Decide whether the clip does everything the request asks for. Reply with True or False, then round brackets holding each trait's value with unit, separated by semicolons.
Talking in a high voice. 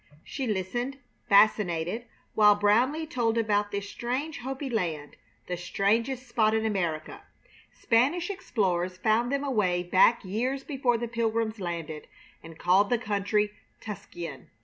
True (215 Hz)